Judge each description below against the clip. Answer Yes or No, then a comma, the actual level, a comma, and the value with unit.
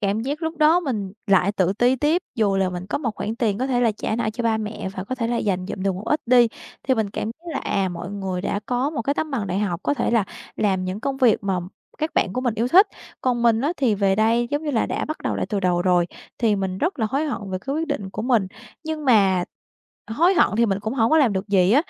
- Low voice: No, high, 225 Hz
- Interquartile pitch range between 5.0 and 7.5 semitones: Yes, average, 5.3 semitones